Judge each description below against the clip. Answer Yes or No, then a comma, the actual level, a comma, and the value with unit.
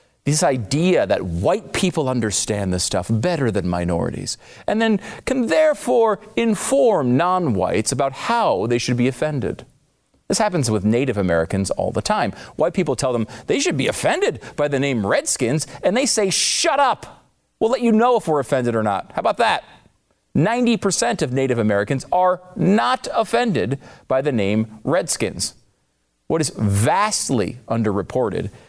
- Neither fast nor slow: Yes, average, 160 wpm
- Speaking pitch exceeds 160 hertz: No, medium, 140 Hz